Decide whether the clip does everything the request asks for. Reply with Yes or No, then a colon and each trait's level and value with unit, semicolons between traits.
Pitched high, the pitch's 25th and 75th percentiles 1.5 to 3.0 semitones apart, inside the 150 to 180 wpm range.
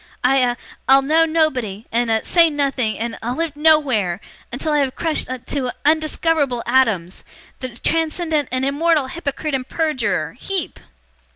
No: very high, 275 Hz; average, 4.2 semitones; average, 155 wpm